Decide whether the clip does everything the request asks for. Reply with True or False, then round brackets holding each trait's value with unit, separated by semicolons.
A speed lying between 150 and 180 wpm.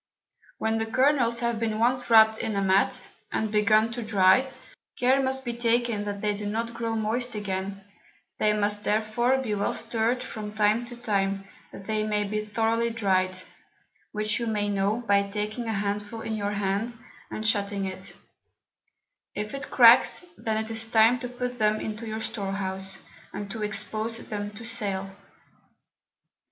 True (170 wpm)